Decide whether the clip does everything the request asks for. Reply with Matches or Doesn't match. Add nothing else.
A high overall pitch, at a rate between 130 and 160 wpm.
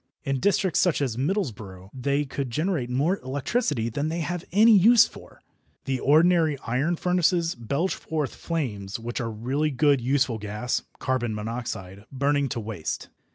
Doesn't match